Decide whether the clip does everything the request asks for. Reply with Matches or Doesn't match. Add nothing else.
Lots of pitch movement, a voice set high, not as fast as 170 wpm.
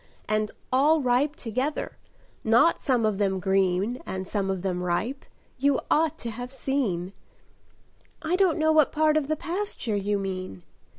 Matches